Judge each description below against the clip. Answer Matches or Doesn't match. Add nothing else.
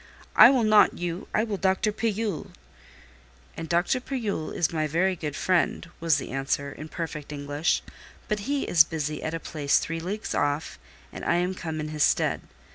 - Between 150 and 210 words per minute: Matches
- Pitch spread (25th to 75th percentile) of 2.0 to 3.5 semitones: Doesn't match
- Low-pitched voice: Doesn't match